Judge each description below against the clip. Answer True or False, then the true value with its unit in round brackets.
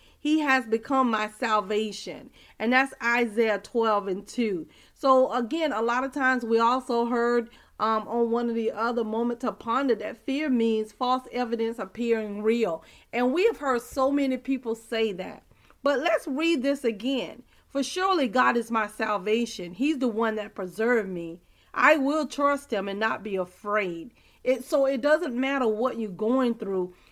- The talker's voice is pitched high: True (235 Hz)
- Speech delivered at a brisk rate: False (175 wpm)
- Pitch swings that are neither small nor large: True (3.3 semitones)